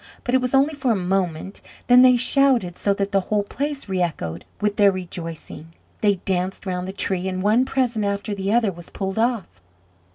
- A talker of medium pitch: No, high, 200 Hz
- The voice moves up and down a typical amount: Yes, average, 4.7 semitones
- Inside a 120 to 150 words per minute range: No, average, 195 wpm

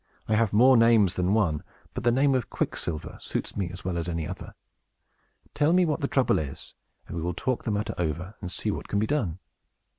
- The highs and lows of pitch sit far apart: Yes, wide, 6.3 semitones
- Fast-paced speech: Yes, fast, 220 wpm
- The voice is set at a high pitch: No, low, 105 Hz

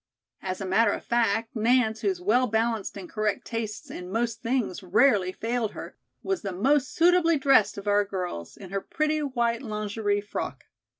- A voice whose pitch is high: Yes, high, 220 Hz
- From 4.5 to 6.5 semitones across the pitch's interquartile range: No, average, 3.6 semitones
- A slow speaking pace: No, average, 175 wpm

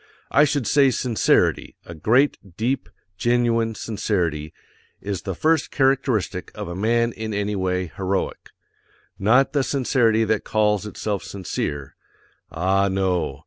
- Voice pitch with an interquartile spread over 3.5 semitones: Yes, average, 4.2 semitones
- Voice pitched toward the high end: No, low, 105 Hz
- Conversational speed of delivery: No, slow, 130 wpm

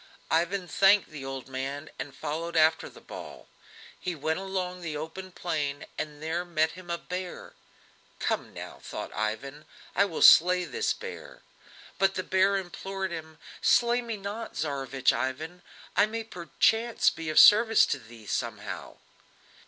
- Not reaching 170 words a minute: Yes, average, 155 wpm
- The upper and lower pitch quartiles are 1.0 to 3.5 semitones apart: No, average, 4.4 semitones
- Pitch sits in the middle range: Yes, medium, 170 Hz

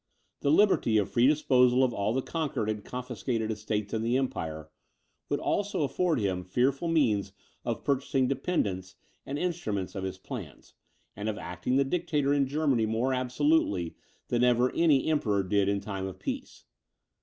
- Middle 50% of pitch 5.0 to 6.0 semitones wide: Yes, wide, 5.6 semitones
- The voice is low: Yes, low, 125 Hz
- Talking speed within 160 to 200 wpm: Yes, average, 165 wpm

